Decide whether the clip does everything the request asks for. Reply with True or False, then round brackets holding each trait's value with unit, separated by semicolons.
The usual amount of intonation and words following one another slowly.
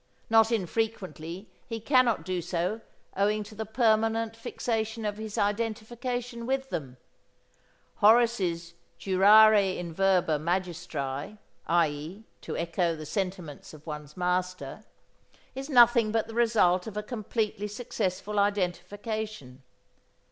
True (4.1 semitones; 115 wpm)